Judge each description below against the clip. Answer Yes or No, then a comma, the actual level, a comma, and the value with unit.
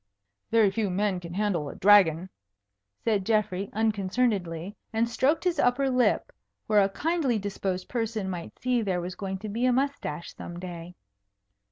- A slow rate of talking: No, average, 160 wpm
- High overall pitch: Yes, high, 205 Hz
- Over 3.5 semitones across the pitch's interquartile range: Yes, average, 4.1 semitones